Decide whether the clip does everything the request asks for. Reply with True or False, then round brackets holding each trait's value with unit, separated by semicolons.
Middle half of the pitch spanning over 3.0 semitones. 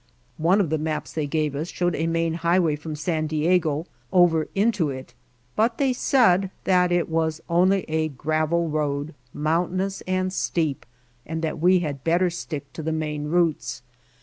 False (2.6 semitones)